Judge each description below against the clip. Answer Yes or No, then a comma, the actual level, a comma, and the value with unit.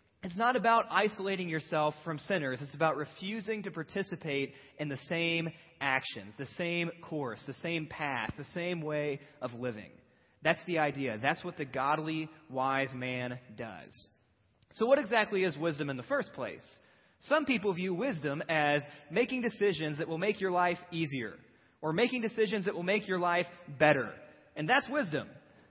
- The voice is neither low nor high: Yes, medium, 160 Hz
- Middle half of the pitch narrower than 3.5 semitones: No, average, 5.3 semitones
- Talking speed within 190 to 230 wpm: No, average, 165 wpm